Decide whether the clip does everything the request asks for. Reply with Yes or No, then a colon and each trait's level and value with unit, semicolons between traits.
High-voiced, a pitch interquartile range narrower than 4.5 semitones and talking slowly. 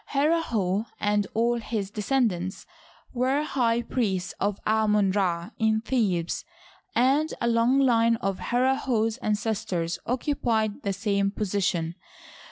Yes: high, 220 Hz; average, 3.5 semitones; slow, 115 wpm